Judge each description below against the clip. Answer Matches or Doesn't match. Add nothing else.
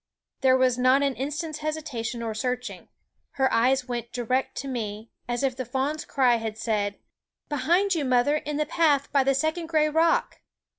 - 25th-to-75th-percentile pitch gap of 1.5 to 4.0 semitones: Matches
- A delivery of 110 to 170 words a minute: Doesn't match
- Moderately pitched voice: Doesn't match